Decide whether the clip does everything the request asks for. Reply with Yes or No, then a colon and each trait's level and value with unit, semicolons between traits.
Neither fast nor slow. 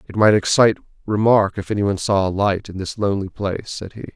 No: fast, 215 wpm